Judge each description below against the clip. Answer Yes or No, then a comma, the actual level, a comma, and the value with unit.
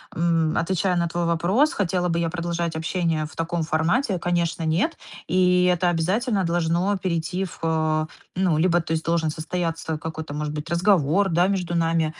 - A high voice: No, medium, 170 Hz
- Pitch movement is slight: Yes, narrow, 1.9 semitones